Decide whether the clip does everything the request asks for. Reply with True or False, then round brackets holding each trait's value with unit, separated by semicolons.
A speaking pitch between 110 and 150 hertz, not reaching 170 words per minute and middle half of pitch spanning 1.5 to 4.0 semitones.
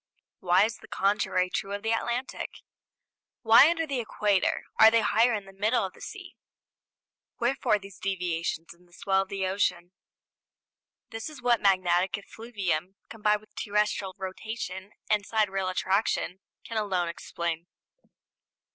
False (200 Hz; 145 wpm; 3.1 semitones)